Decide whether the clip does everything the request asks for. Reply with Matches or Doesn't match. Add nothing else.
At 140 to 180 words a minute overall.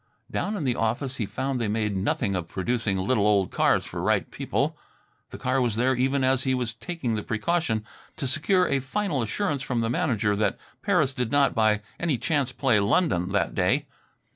Doesn't match